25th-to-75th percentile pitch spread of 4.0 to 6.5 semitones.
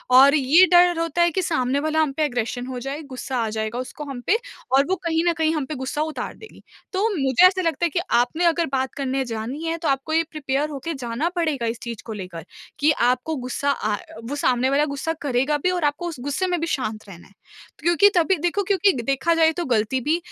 Yes: average, 4.6 semitones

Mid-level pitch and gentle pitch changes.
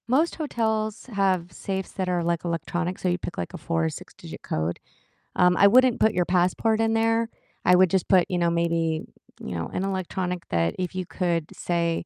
No: medium, 180 Hz; average, 3.0 semitones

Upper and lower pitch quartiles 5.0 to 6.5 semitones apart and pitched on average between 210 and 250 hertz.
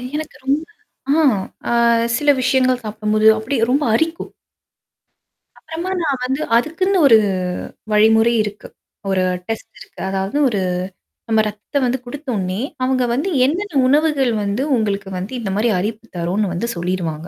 Yes: wide, 5.4 semitones; high, 230 Hz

